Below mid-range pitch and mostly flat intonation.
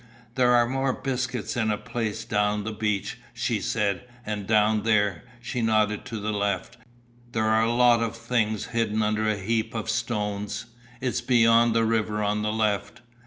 Yes: low, 110 Hz; narrow, 1.9 semitones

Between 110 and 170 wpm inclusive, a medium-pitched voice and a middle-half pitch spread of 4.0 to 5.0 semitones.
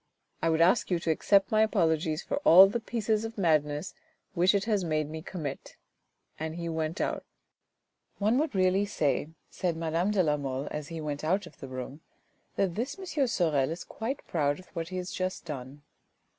No: average, 200 wpm; medium, 170 Hz; average, 4.6 semitones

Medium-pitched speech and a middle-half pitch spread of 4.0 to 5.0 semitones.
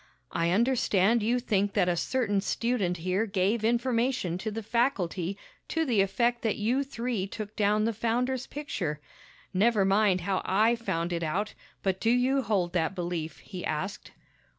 No: high, 210 Hz; average, 4.3 semitones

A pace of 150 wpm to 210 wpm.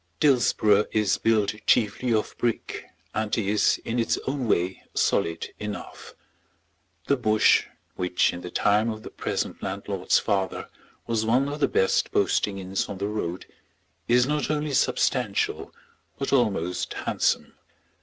No: average, 140 wpm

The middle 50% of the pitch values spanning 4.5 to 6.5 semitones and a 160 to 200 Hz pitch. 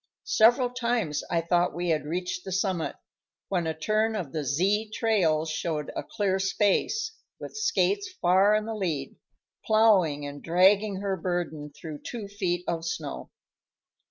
Yes: average, 4.8 semitones; medium, 185 Hz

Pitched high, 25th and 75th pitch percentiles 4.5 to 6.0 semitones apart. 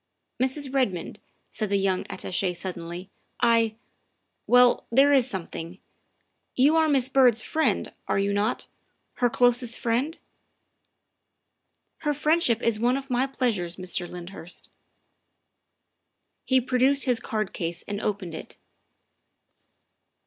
Yes: high, 235 Hz; wide, 5.5 semitones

